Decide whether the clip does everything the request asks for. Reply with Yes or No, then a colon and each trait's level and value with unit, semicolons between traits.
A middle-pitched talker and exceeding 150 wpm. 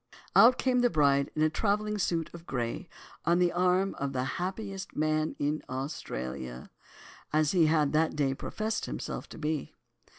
Yes: medium, 155 Hz; average, 160 wpm